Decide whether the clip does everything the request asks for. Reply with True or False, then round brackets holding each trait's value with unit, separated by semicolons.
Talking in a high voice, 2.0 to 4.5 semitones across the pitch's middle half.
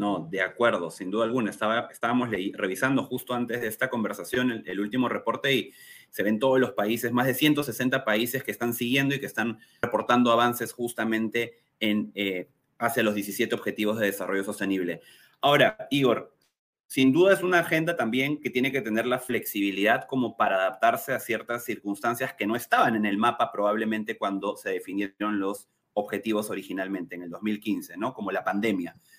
False (115 Hz; 3.8 semitones)